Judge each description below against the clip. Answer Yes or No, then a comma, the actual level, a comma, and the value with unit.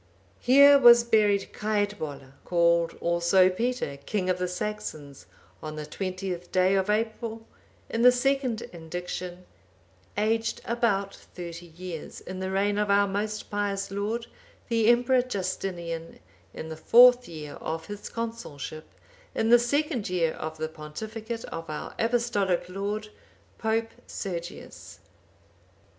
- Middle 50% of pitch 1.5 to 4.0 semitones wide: No, average, 4.8 semitones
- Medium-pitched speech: No, high, 200 Hz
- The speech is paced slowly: Yes, slow, 130 wpm